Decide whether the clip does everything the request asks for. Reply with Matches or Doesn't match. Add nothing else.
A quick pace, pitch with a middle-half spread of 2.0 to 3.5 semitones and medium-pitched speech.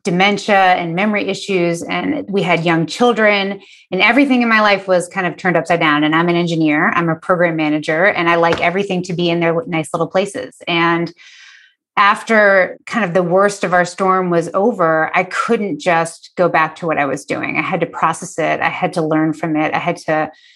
Matches